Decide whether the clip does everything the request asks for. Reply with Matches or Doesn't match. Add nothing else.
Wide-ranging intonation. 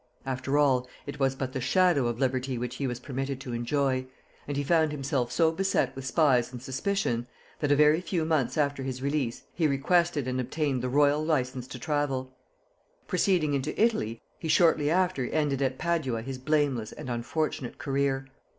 Doesn't match